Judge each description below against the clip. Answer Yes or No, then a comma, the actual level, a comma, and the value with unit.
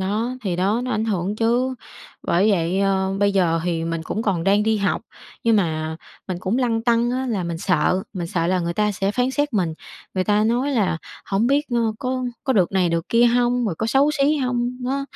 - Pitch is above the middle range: Yes, high, 210 Hz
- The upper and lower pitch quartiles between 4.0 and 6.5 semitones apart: Yes, average, 4.9 semitones